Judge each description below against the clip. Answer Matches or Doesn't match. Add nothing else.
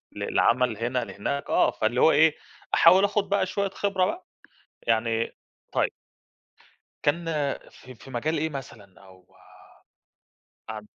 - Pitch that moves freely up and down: Matches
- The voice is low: Matches